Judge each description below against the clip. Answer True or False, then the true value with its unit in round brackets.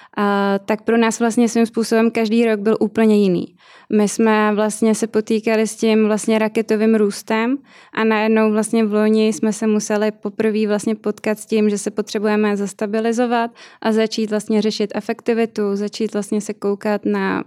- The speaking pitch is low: False (220 Hz)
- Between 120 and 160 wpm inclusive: False (170 wpm)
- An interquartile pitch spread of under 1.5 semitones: True (1.0 semitones)